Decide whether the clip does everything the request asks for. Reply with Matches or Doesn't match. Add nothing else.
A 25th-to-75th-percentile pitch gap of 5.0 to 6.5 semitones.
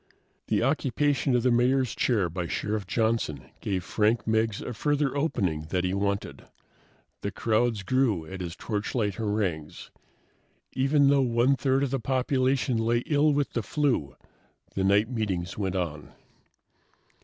Matches